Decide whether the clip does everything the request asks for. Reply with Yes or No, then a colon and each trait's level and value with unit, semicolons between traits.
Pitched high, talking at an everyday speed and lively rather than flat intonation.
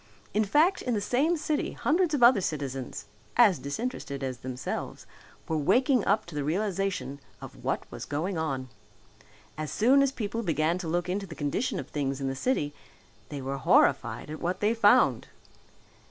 No: medium, 180 Hz; average, 175 wpm; wide, 8.6 semitones